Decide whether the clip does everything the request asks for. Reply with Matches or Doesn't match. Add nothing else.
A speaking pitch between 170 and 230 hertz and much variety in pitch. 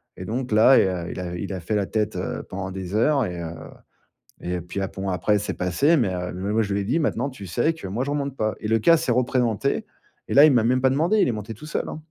Doesn't match